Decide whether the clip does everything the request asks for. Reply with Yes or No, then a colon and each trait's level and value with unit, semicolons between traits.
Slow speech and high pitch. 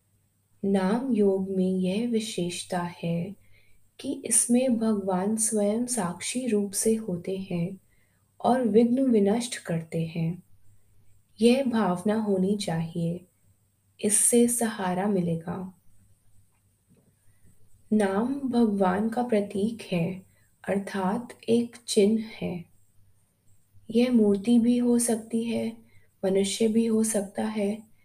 Yes: slow, 100 wpm; high, 195 Hz